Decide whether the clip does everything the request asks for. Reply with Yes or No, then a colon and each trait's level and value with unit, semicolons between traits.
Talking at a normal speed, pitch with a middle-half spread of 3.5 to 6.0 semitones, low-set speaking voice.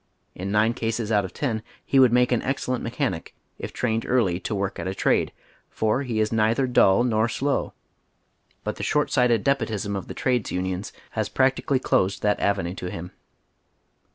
Yes: average, 180 wpm; average, 4.1 semitones; low, 110 Hz